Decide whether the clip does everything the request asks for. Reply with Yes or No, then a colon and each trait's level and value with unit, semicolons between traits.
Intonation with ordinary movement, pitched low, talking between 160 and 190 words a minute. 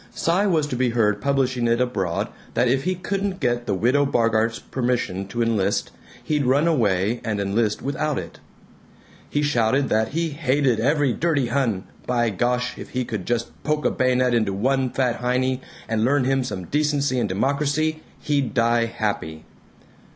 Yes: average, 3.9 semitones; low, 125 Hz; average, 175 wpm